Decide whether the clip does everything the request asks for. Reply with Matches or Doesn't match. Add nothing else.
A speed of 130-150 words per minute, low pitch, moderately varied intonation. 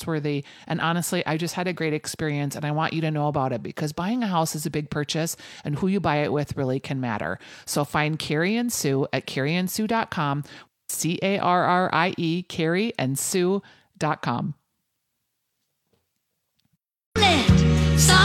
Doesn't match